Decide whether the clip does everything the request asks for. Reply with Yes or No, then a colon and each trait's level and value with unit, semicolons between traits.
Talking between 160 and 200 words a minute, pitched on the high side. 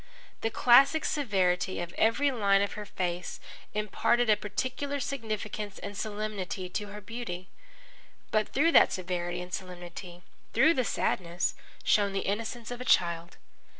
No: average, 145 wpm; high, 205 Hz